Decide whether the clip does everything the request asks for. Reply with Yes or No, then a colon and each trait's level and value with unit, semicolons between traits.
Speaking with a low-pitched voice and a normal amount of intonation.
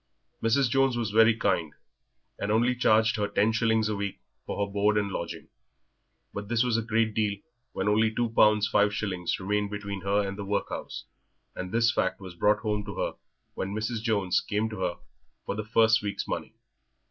No: low, 105 Hz; narrow, 1.8 semitones